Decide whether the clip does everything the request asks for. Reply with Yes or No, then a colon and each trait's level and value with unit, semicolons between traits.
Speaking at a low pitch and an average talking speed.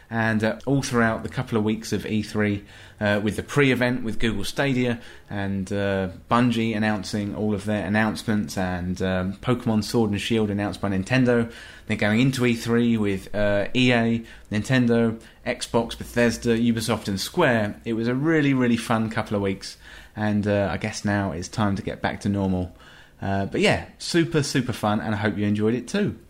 Yes: low, 110 Hz; average, 185 wpm